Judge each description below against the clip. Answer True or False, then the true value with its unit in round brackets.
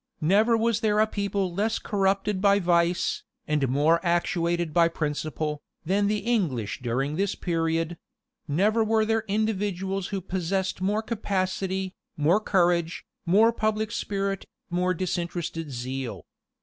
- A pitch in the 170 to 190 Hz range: True (185 Hz)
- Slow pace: True (130 wpm)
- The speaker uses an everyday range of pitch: True (3.7 semitones)